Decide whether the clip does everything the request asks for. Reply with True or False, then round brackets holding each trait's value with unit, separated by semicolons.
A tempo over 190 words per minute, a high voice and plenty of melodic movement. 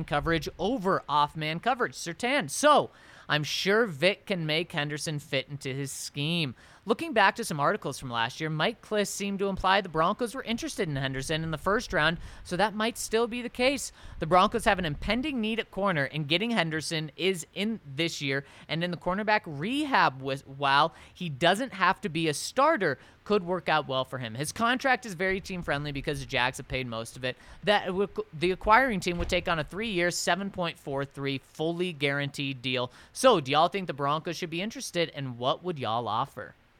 False (200 wpm; 170 Hz; 6.1 semitones)